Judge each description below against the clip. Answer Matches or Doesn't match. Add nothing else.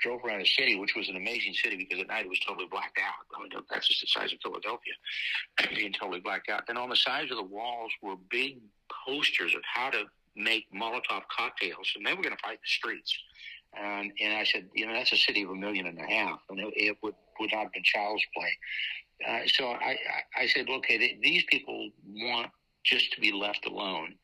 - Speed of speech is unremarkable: Doesn't match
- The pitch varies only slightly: Matches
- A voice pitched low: Matches